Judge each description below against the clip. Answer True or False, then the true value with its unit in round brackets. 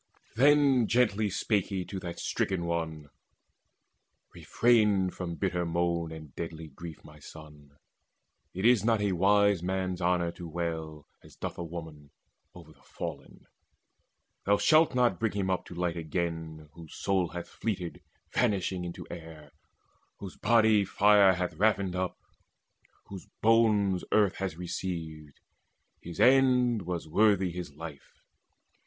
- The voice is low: True (90 Hz)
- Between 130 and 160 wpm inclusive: True (140 wpm)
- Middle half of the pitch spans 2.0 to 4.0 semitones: True (3.6 semitones)